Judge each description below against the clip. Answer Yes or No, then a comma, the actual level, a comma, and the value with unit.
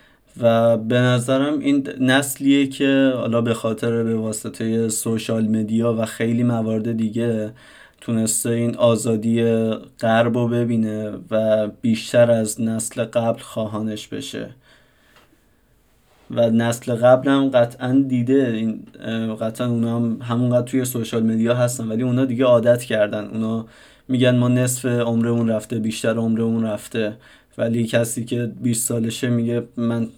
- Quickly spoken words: No, average, 130 wpm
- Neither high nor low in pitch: No, low, 115 Hz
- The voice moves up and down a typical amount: No, narrow, 1.5 semitones